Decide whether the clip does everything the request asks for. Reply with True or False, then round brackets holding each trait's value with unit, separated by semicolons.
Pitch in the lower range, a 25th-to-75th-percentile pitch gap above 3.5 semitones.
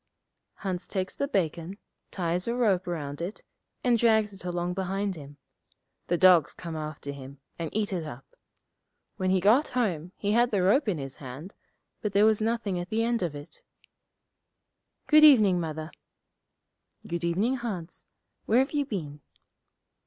False (185 Hz; 4.8 semitones)